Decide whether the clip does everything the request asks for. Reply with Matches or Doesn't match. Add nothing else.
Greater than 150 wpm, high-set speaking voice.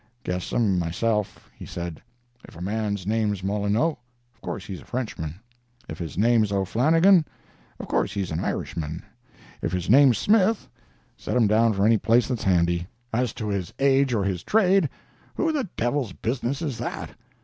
Doesn't match